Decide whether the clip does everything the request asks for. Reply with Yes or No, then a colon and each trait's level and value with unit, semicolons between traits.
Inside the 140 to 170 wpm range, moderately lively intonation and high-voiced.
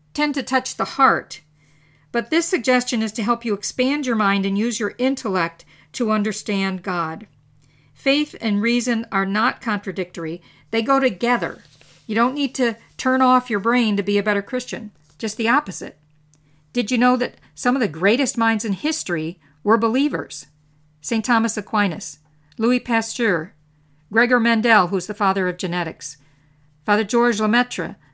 No: average, 160 wpm; wide, 6.2 semitones; high, 210 Hz